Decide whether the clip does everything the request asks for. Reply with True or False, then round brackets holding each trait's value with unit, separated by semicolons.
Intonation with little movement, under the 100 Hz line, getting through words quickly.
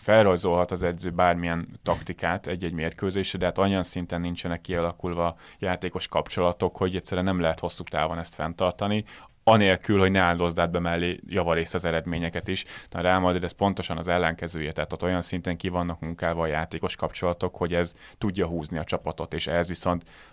True (1.3 semitones; 90 Hz; 170 wpm)